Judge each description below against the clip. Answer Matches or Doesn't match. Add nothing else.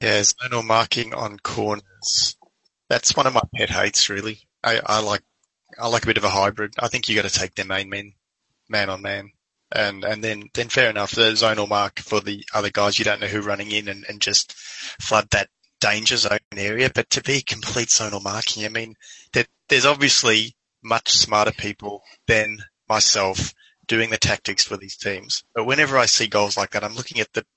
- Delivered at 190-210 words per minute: Matches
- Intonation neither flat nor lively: Doesn't match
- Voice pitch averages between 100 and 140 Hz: Matches